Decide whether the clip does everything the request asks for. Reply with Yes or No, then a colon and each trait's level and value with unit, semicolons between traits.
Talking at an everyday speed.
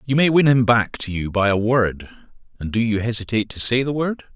No: fast, 235 wpm